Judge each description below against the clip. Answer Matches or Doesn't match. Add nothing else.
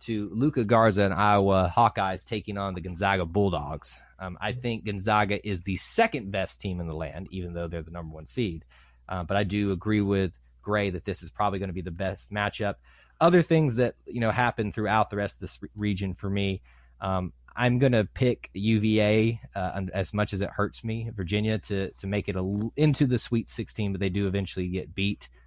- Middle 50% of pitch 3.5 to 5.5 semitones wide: Doesn't match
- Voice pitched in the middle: Doesn't match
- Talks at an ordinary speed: Doesn't match